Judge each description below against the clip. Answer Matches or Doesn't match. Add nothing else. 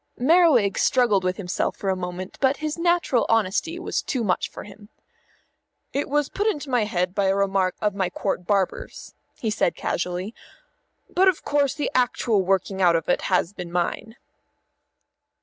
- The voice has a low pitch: Doesn't match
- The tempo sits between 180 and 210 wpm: Doesn't match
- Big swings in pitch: Matches